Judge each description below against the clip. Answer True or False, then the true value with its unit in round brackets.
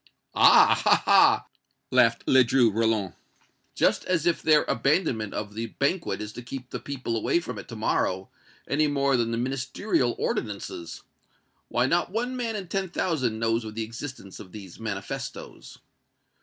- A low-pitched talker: True (120 Hz)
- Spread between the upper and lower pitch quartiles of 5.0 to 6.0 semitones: True (5.6 semitones)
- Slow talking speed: False (160 wpm)